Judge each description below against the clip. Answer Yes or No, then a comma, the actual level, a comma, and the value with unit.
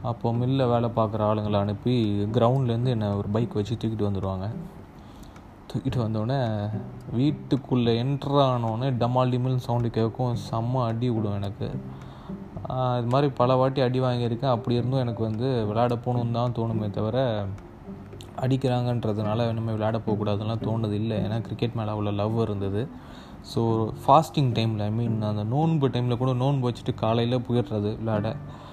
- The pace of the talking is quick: Yes, fast, 135 wpm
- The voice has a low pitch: Yes, low, 115 Hz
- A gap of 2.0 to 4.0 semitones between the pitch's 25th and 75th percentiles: Yes, average, 2.8 semitones